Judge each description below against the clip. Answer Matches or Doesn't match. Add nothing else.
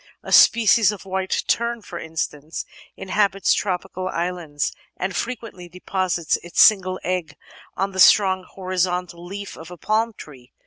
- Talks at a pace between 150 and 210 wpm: Doesn't match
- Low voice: Doesn't match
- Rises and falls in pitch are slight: Matches